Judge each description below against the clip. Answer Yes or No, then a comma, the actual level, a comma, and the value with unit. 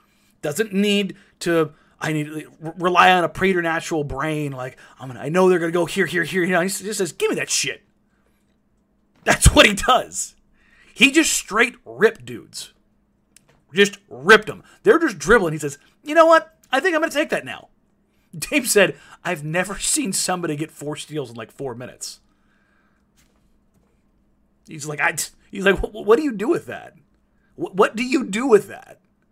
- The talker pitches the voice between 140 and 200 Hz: Yes, high, 190 Hz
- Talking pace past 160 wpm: Yes, average, 185 wpm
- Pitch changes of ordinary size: No, wide, 6.7 semitones